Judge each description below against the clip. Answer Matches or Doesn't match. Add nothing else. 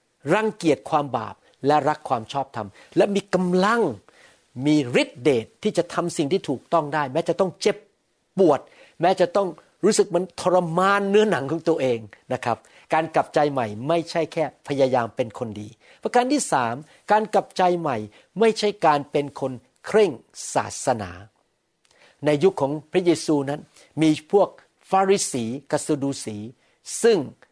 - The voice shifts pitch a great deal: Matches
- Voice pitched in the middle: Matches